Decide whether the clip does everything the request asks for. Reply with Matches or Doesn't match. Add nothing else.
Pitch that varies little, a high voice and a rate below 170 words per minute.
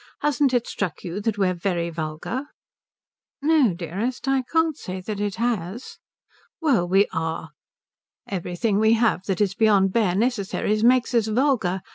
Doesn't match